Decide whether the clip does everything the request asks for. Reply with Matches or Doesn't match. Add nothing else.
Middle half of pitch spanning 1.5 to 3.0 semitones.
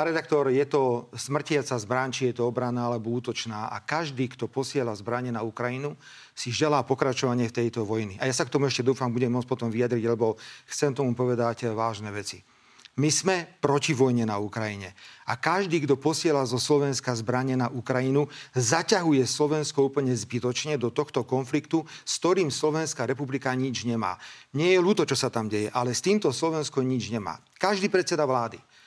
Doesn't match